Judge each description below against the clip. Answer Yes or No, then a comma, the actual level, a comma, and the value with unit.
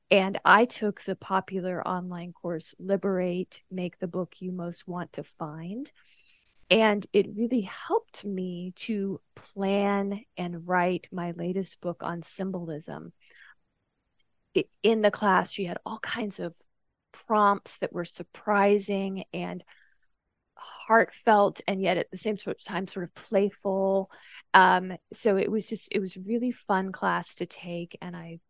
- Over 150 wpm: No, average, 145 wpm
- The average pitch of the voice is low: No, high, 190 Hz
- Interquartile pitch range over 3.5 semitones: No, narrow, 2.6 semitones